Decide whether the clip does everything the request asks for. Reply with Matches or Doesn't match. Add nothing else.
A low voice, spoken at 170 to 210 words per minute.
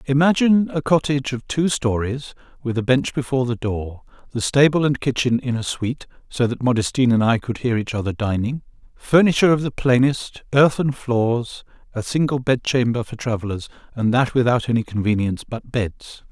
Matches